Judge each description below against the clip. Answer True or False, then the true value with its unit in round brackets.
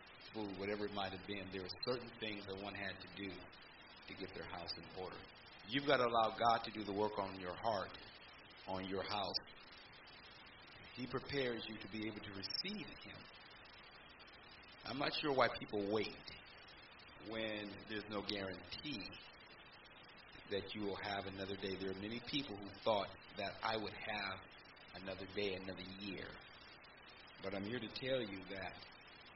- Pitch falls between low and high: False (100 Hz)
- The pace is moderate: True (170 wpm)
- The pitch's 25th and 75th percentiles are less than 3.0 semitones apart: True (2.4 semitones)